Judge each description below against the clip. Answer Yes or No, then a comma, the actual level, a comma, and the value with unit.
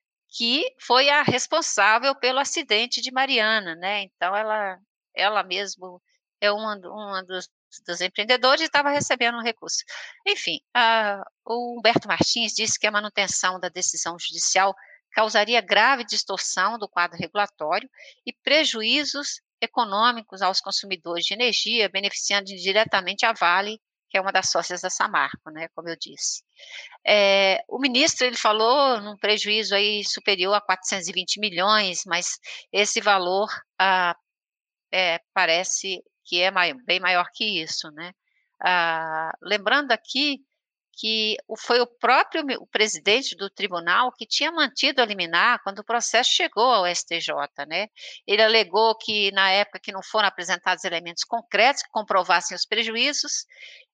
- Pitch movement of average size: Yes, average, 4.6 semitones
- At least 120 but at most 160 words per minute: Yes, average, 140 wpm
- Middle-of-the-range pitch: No, high, 210 Hz